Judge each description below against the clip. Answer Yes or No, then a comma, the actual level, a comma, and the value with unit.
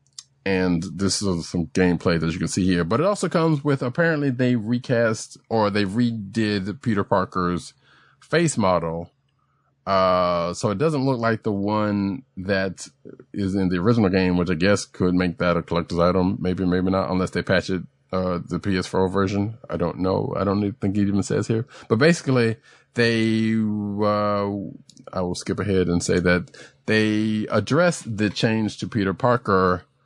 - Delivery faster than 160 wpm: Yes, average, 175 wpm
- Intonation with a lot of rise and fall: No, average, 3.8 semitones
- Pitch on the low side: Yes, low, 100 Hz